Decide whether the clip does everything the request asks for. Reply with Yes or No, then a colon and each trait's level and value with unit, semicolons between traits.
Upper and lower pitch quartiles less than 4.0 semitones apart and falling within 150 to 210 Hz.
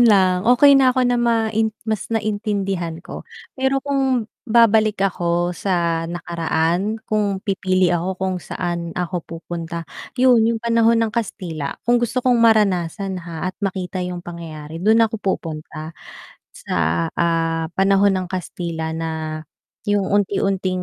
No: average, 4.5 semitones; high, 190 Hz